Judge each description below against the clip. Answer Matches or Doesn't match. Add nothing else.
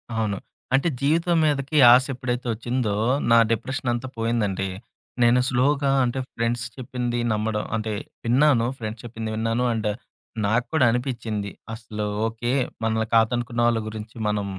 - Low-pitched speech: Matches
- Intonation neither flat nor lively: Doesn't match